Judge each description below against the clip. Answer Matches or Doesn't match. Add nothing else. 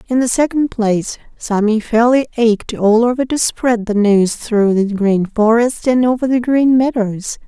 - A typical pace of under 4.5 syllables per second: Matches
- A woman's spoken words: Matches